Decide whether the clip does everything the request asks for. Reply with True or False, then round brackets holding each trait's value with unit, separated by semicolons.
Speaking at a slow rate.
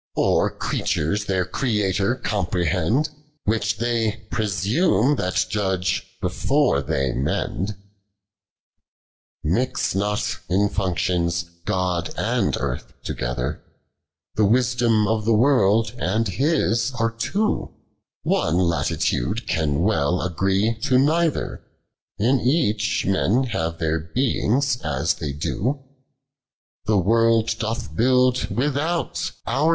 True (100 wpm)